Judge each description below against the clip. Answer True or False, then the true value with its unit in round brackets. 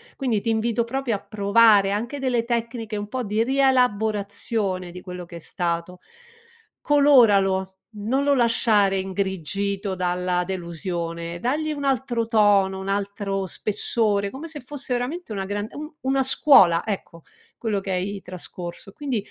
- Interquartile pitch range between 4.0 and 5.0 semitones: True (4.3 semitones)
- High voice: True (205 Hz)